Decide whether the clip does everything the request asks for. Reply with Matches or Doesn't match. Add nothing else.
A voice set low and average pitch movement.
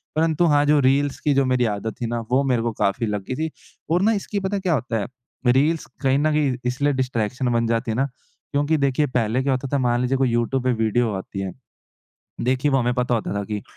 Matches